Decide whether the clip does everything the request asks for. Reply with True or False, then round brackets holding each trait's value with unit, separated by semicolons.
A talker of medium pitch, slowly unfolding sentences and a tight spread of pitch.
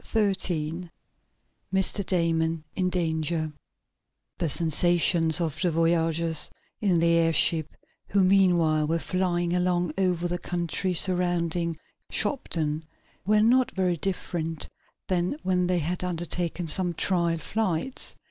True (175 Hz; 120 wpm; 1.9 semitones)